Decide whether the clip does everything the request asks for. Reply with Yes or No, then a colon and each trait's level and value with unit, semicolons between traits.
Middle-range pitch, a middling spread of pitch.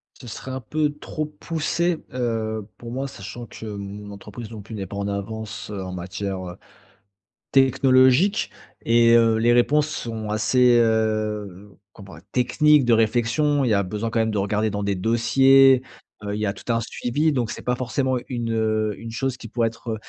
No: low, 115 Hz; average, 3.5 semitones